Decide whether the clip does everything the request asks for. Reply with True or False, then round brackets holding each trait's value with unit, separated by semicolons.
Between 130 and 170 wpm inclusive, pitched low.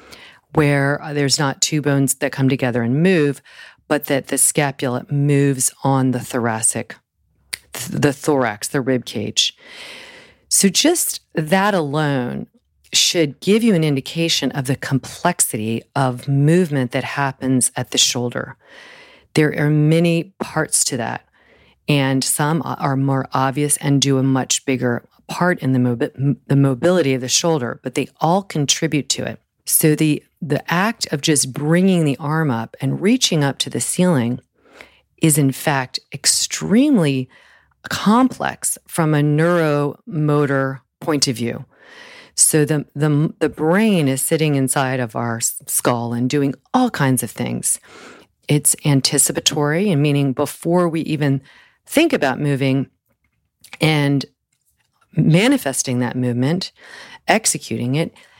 False (135 wpm; 145 Hz)